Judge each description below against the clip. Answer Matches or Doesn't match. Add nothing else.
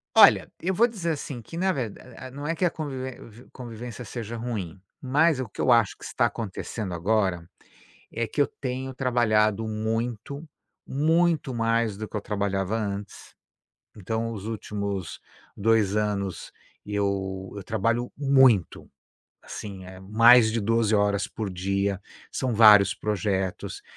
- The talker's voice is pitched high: Doesn't match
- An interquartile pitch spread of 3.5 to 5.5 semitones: Matches